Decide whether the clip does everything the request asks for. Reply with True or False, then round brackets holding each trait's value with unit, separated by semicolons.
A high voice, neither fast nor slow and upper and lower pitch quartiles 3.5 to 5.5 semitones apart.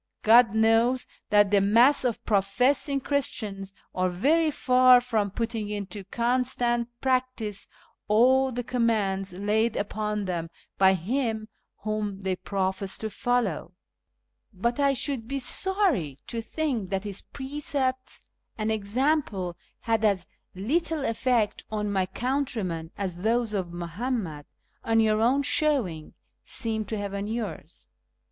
False (220 Hz; 130 wpm; 4.3 semitones)